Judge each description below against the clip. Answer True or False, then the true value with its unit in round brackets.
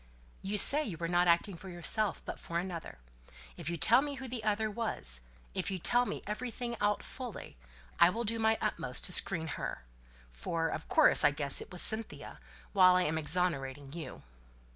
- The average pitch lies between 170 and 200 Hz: True (185 Hz)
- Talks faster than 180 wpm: True (190 wpm)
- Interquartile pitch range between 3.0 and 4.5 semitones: False (5.3 semitones)